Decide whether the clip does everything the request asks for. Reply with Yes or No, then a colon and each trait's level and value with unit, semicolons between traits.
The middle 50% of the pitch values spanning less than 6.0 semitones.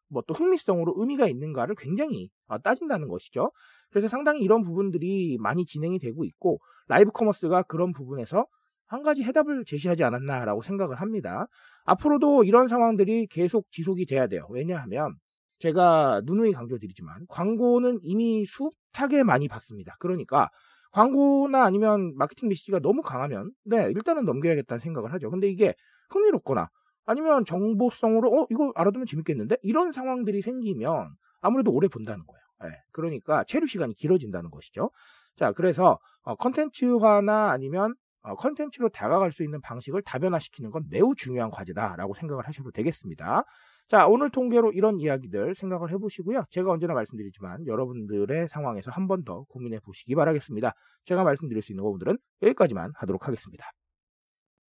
No: wide, 8.1 semitones